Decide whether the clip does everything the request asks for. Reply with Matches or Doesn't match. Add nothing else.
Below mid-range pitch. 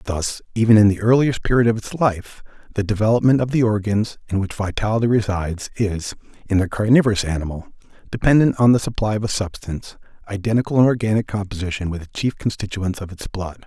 Matches